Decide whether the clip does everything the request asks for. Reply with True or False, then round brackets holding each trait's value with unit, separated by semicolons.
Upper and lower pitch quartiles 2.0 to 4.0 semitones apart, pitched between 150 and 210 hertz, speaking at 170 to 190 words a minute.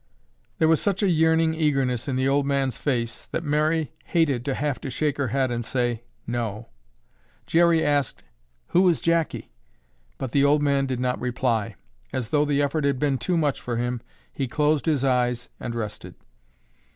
False (3.7 semitones; 140 Hz; 180 wpm)